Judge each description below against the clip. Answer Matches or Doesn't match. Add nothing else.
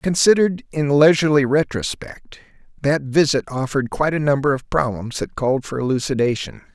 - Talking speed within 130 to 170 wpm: Matches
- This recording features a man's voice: Matches